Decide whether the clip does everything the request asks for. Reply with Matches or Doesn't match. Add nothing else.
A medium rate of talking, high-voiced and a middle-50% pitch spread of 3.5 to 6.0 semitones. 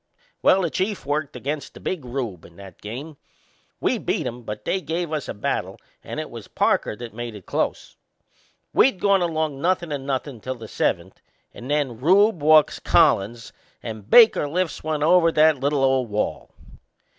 Doesn't match